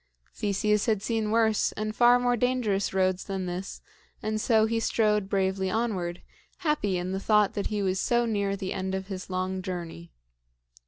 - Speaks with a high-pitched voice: Yes, high, 200 Hz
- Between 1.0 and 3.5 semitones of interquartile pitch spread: Yes, average, 2.7 semitones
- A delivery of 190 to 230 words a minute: No, average, 175 wpm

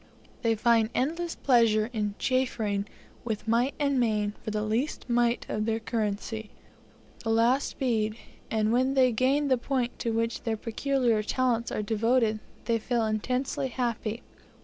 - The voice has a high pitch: Yes, high, 230 Hz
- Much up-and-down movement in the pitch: No, average, 2.7 semitones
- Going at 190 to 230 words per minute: No, average, 150 wpm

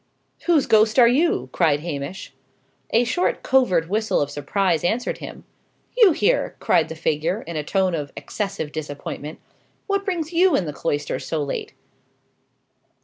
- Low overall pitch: No, medium, 185 Hz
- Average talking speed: Yes, average, 150 wpm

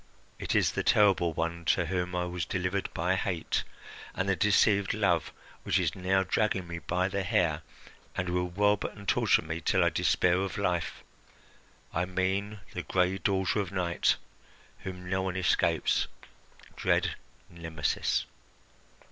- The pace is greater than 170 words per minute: No, average, 150 wpm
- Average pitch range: No, narrow, 1.8 semitones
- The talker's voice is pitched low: Yes, very low, 90 Hz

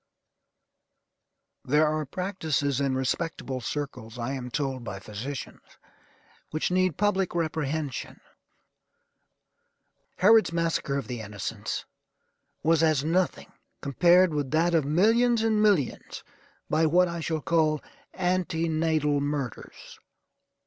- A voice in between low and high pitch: Yes, medium, 155 Hz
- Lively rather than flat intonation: No, average, 4.2 semitones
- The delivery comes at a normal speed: No, slow, 110 wpm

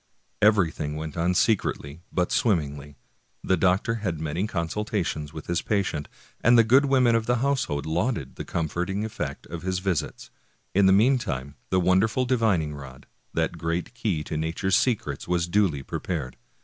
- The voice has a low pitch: Yes, very low, 90 Hz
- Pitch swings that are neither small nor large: No, wide, 5.7 semitones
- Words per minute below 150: No, average, 160 wpm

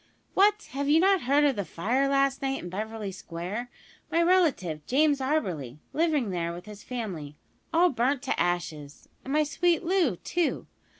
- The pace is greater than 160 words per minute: Yes, average, 170 wpm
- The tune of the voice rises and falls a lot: Yes, wide, 9.0 semitones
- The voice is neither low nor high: No, very high, 260 Hz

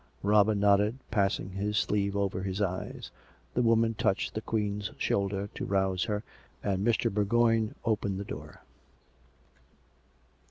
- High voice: No, low, 100 Hz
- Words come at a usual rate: No, slow, 130 wpm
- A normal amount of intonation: No, narrow, 1.7 semitones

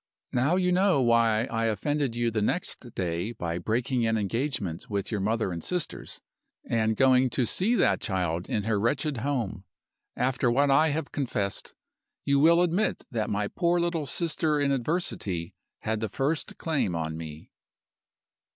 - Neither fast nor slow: Yes, average, 160 wpm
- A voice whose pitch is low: Yes, low, 120 Hz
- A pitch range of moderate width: No, wide, 6.0 semitones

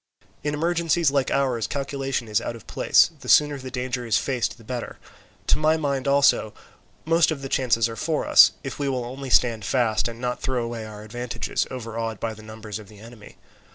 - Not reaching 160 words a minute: No, fast, 205 wpm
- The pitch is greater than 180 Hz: No, low, 125 Hz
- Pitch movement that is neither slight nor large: Yes, average, 3.4 semitones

